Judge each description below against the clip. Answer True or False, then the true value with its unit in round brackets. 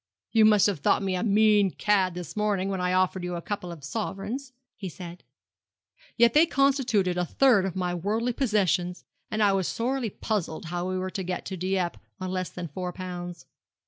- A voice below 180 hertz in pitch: False (190 Hz)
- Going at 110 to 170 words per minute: False (200 wpm)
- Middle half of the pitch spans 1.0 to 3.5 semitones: True (3.1 semitones)